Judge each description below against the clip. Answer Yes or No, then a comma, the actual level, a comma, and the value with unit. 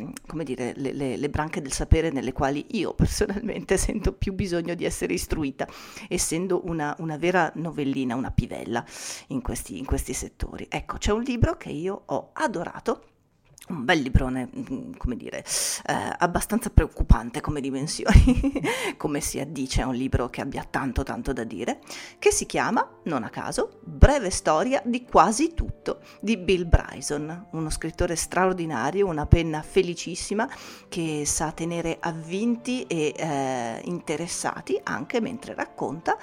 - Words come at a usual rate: Yes, average, 150 wpm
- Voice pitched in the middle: Yes, medium, 165 Hz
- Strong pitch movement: Yes, wide, 5.7 semitones